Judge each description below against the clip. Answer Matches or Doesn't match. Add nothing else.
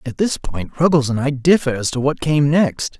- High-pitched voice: Doesn't match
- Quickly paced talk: Matches